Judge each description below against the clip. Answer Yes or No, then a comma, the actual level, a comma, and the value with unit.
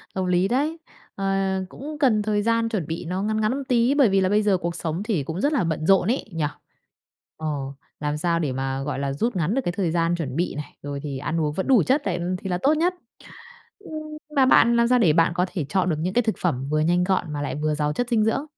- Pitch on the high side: No, medium, 180 Hz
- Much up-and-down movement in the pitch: Yes, wide, 6.6 semitones